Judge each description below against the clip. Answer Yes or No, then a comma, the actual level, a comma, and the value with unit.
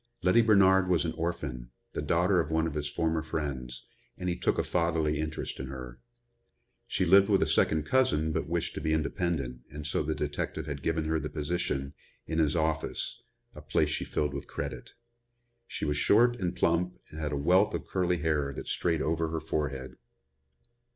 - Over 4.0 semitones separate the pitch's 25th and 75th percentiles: No, average, 3.1 semitones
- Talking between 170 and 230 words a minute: Yes, average, 190 wpm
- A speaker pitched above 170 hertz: No, very low, 80 Hz